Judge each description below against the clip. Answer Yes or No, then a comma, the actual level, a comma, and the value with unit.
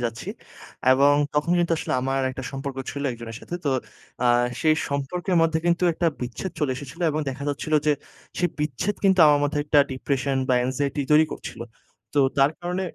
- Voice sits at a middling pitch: Yes, medium, 145 Hz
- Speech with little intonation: No, average, 3.5 semitones